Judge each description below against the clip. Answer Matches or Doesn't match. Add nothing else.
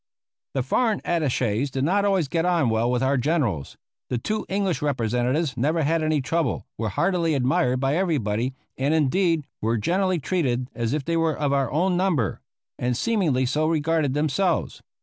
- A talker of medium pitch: Matches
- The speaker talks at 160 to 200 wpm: Matches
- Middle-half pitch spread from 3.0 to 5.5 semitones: Matches